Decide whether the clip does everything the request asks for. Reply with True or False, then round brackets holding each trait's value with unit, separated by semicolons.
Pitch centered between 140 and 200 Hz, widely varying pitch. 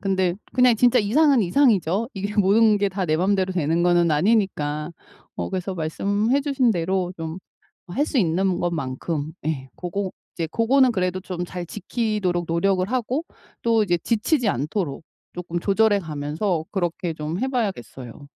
False (185 Hz; 4.4 semitones)